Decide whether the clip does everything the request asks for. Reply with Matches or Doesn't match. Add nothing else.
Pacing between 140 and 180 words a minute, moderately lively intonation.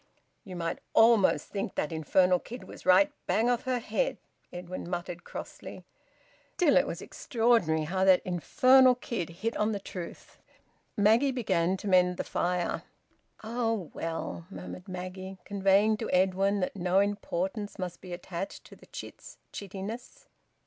Matches